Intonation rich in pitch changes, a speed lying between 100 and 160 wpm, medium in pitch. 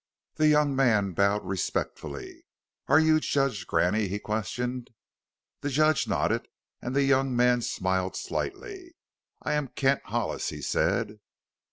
No: wide, 5.7 semitones; slow, 135 wpm; low, 125 Hz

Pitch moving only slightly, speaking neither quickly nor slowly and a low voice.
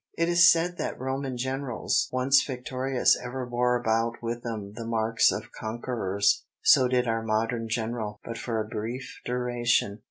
Yes: narrow, 2.3 semitones; average, 160 wpm; low, 120 Hz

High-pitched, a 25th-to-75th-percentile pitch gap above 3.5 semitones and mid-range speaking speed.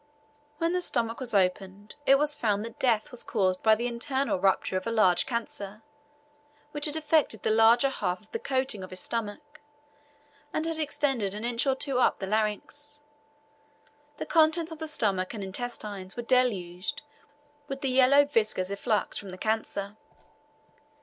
Yes: high, 230 Hz; wide, 5.4 semitones; average, 170 wpm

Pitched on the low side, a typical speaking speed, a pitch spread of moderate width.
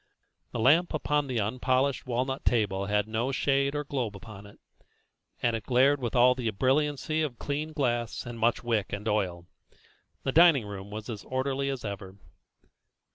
Yes: low, 125 Hz; average, 165 wpm; average, 4.4 semitones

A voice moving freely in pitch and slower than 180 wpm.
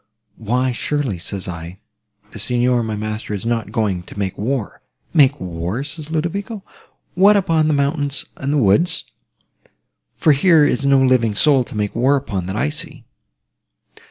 Yes: wide, 5.8 semitones; average, 160 wpm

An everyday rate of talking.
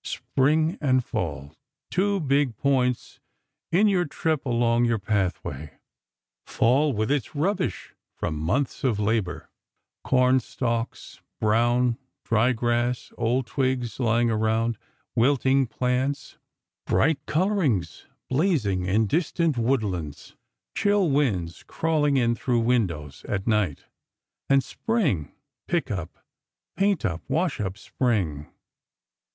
No: slow, 110 wpm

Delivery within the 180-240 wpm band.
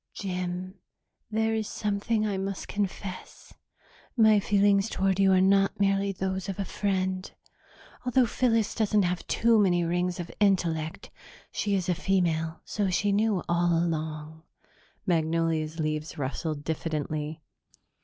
No: slow, 135 wpm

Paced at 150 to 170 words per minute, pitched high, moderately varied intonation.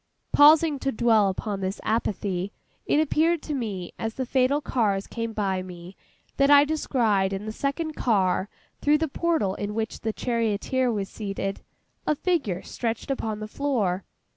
No: average, 165 wpm; high, 225 Hz; wide, 6.0 semitones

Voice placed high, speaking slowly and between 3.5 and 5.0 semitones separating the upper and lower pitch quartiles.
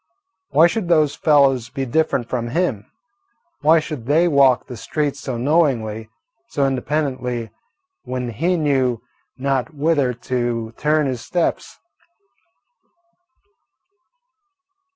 No: low, 135 Hz; slow, 110 wpm; average, 4.0 semitones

